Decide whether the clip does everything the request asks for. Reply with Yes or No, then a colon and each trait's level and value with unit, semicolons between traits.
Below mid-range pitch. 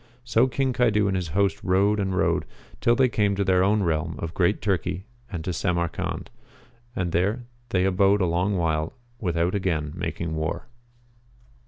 Yes: very low, 95 Hz